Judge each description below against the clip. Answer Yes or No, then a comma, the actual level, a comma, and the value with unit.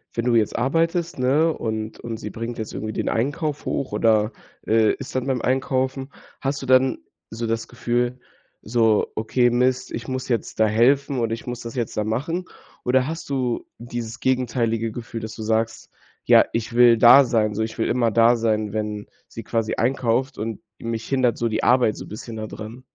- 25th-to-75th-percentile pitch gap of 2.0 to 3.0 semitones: Yes, narrow, 2.6 semitones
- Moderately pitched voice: No, low, 120 Hz